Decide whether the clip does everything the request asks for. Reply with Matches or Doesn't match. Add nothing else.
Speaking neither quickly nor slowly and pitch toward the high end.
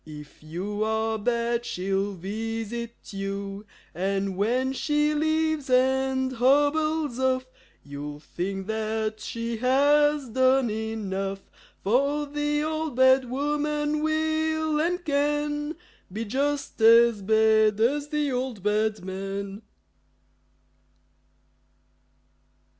Doesn't match